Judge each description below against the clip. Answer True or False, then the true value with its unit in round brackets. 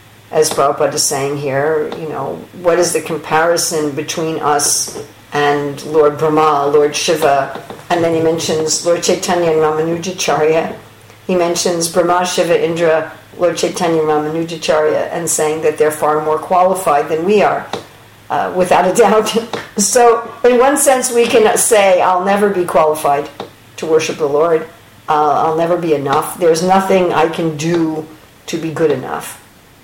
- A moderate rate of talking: True (155 wpm)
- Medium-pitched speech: True (160 Hz)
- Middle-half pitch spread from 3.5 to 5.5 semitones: False (2.8 semitones)